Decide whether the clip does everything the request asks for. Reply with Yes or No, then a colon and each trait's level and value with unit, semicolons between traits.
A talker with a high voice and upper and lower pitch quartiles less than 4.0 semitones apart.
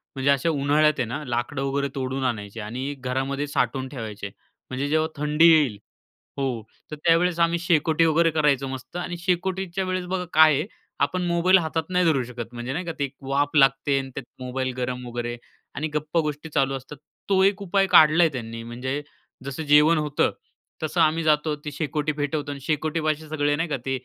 No: medium, 145 Hz; average, 3.4 semitones